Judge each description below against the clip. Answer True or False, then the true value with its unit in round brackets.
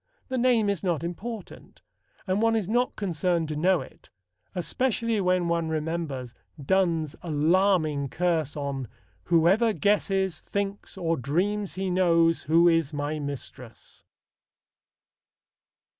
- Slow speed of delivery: True (120 wpm)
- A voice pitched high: False (175 Hz)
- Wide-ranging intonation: False (4.2 semitones)